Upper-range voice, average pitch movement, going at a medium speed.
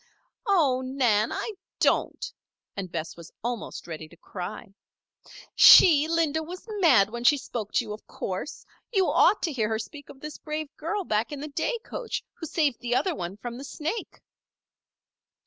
No: very high, 270 Hz; wide, 6.8 semitones; average, 175 wpm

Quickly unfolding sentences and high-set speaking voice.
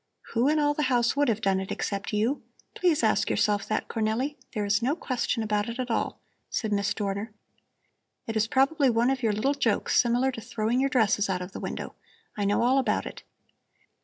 Yes: fast, 210 wpm; high, 230 Hz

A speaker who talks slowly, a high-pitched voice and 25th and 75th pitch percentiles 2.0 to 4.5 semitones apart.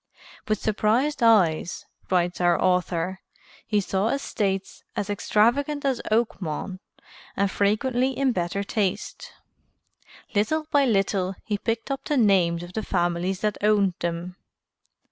Yes: slow, 125 wpm; high, 205 Hz; average, 4.0 semitones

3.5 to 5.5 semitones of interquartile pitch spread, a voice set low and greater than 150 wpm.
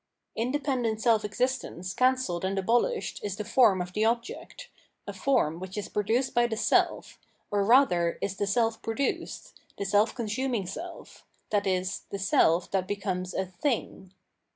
No: average, 4.3 semitones; high, 210 Hz; average, 160 wpm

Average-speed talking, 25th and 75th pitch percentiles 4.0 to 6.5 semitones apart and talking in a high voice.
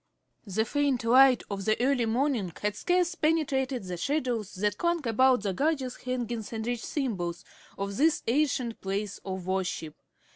Yes: average, 155 wpm; average, 5.2 semitones; high, 240 Hz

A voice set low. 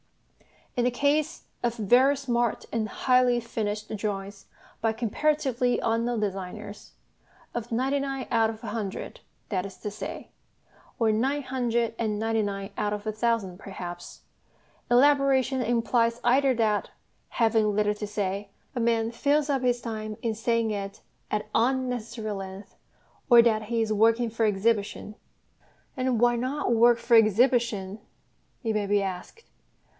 No: high, 230 Hz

